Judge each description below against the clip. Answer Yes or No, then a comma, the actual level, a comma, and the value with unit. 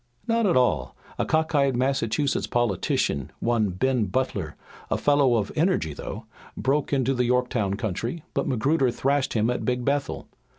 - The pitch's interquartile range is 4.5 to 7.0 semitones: No, average, 4.1 semitones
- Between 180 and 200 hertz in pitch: No, low, 125 Hz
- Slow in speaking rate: No, average, 160 wpm